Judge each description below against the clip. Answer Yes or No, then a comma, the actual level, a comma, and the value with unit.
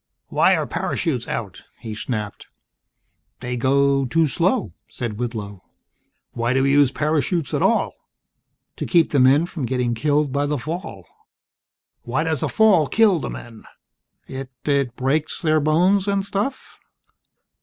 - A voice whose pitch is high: No, medium, 140 Hz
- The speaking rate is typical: Yes, average, 145 wpm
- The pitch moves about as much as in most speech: Yes, average, 4.8 semitones